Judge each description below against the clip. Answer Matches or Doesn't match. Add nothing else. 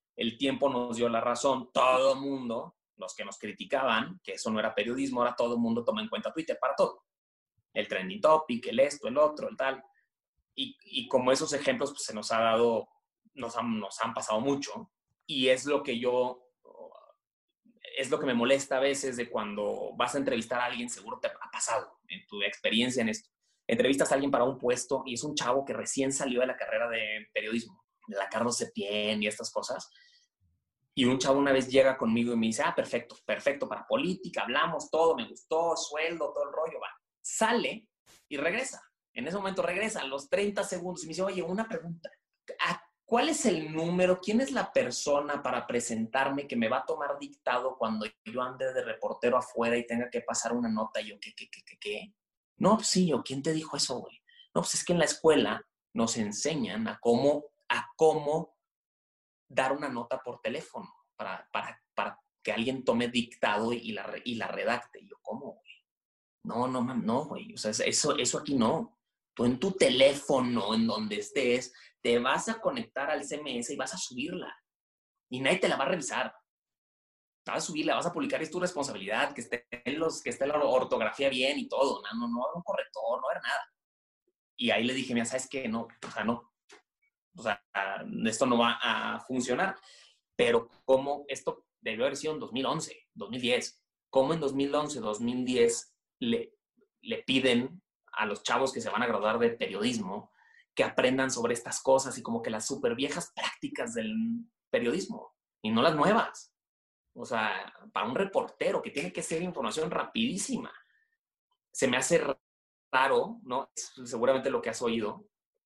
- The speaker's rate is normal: Doesn't match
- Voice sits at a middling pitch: Matches